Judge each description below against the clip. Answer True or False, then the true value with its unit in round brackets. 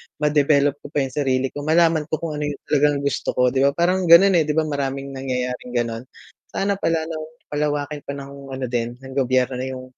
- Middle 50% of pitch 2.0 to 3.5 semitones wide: True (2.9 semitones)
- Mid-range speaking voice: True (145 Hz)